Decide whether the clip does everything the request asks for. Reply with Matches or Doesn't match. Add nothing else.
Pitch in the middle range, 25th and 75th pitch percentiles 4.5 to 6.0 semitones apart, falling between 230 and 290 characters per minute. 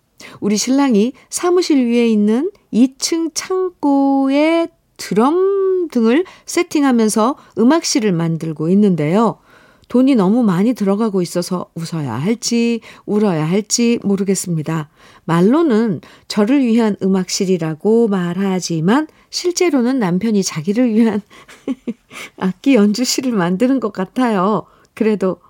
Doesn't match